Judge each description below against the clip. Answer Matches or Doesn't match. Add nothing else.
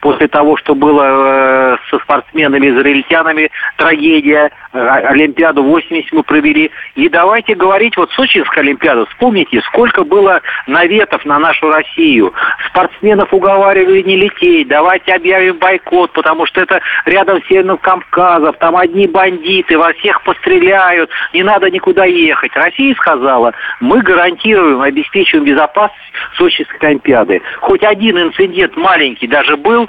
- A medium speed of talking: Matches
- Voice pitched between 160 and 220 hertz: Matches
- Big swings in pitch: Matches